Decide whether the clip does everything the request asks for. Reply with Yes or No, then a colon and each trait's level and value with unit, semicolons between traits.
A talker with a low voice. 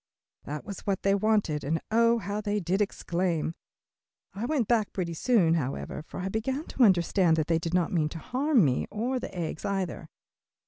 No: high, 190 Hz